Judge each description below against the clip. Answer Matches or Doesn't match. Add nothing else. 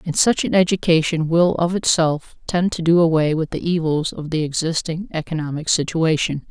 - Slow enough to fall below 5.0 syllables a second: Doesn't match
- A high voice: Doesn't match